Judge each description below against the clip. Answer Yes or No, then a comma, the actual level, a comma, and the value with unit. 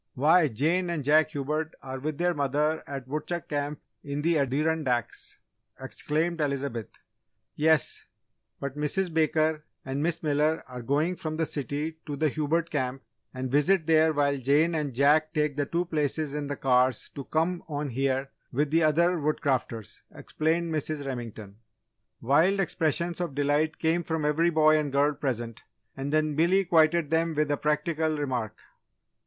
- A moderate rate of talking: Yes, average, 160 wpm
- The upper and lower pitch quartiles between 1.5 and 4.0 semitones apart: Yes, narrow, 2.4 semitones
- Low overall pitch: No, medium, 150 Hz